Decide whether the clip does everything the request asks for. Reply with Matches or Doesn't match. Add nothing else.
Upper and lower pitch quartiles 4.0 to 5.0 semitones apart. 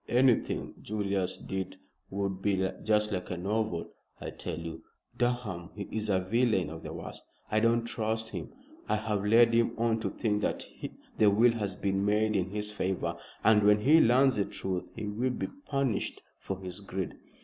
Doesn't match